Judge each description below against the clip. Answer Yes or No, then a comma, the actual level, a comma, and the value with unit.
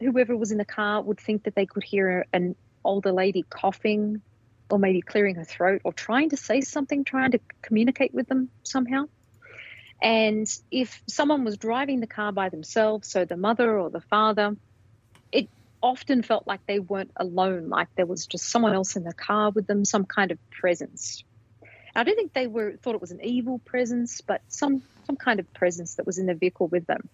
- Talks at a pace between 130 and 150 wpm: No, fast, 205 wpm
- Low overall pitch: No, high, 210 Hz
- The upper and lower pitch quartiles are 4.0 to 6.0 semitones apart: Yes, average, 4.8 semitones